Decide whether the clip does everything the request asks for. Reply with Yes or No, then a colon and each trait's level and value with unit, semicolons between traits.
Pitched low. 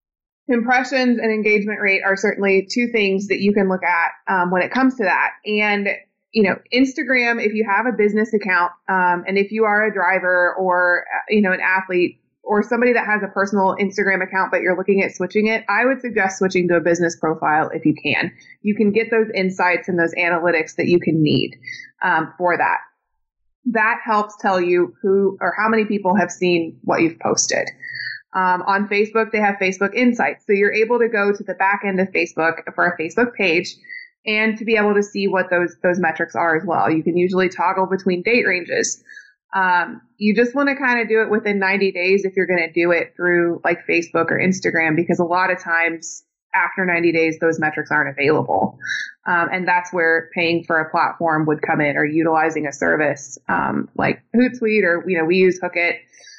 No: high, 190 Hz